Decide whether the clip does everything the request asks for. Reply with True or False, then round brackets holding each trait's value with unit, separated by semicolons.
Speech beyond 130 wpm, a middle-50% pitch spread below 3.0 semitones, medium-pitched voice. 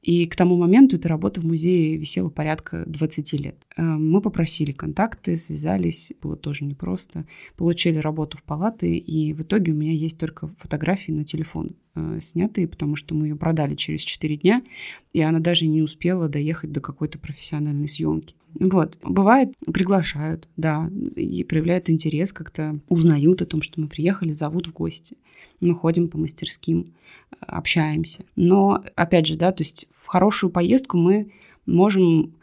True (155 wpm; 2.6 semitones; 160 Hz)